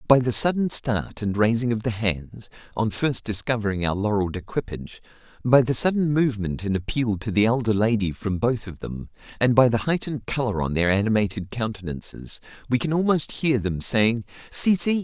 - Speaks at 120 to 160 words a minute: No, average, 170 wpm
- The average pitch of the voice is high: No, low, 115 Hz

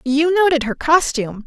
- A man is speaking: No, female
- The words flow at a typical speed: Yes, average, 165 wpm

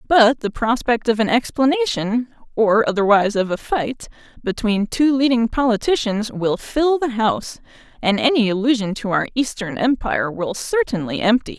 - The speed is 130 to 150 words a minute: Yes, average, 145 wpm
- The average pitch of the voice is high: Yes, high, 230 Hz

